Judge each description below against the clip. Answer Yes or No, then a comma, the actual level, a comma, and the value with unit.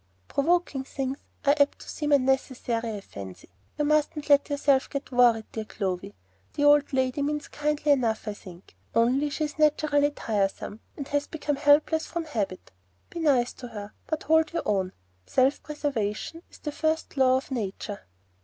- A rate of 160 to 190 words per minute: Yes, average, 165 wpm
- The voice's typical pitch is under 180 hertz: No, very high, 275 Hz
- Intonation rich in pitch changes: No, average, 4.7 semitones